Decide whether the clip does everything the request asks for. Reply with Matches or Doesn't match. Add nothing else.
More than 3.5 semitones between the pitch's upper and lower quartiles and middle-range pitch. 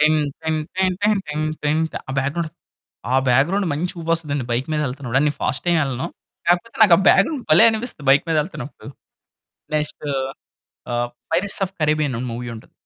Matches